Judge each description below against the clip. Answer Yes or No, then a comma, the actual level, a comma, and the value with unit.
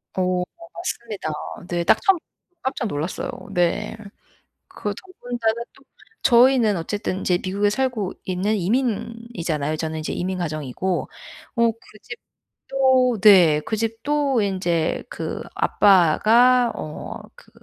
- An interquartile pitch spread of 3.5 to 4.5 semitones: No, average, 5.3 semitones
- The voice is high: Yes, high, 210 Hz